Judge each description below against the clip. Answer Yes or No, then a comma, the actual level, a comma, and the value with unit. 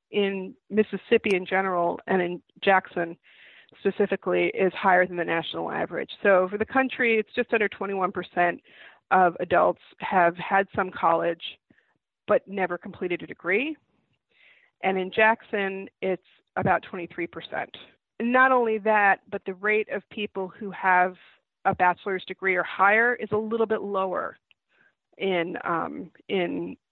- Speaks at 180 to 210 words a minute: No, average, 140 wpm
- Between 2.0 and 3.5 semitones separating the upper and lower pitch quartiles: Yes, average, 2.9 semitones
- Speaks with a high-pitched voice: Yes, high, 195 Hz